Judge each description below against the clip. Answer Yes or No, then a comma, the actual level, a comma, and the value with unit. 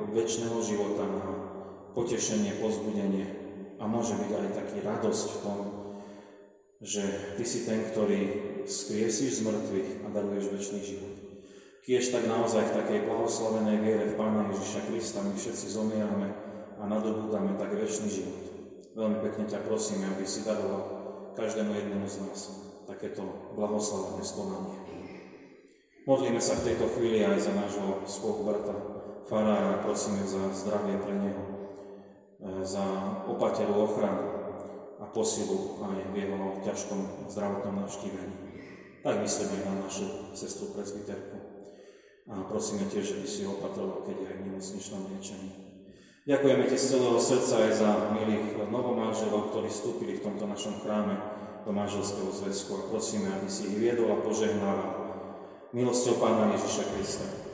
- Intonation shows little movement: Yes, narrow, 1.4 semitones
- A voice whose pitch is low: Yes, low, 105 Hz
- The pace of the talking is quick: No, average, 140 wpm